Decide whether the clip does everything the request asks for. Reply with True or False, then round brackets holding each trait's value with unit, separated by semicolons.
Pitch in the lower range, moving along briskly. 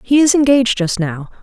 False (230 Hz; 210 wpm)